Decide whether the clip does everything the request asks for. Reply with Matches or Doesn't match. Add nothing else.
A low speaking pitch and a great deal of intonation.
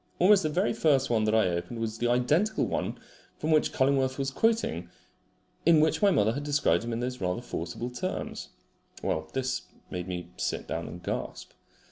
Matches